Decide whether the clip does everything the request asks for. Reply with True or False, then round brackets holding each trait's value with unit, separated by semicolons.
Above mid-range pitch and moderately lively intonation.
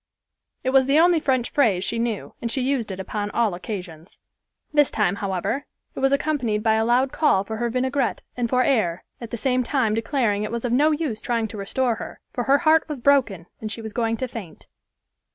True (235 Hz; 4.1 semitones)